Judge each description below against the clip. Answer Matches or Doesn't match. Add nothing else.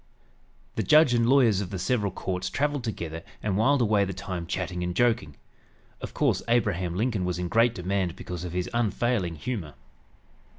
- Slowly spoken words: Doesn't match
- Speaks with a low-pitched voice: Matches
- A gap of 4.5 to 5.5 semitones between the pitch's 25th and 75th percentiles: Matches